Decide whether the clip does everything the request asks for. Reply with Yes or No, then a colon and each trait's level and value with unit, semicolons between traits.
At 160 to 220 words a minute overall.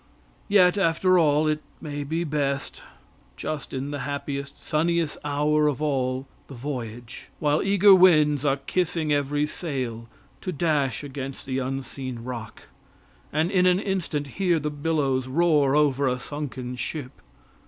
No: average, 145 wpm